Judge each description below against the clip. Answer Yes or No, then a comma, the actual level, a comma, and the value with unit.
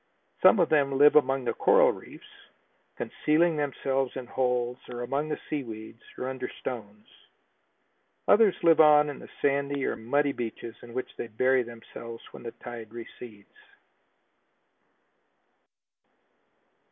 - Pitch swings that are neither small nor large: Yes, average, 3.4 semitones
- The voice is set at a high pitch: No, low, 130 Hz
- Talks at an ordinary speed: No, slow, 130 wpm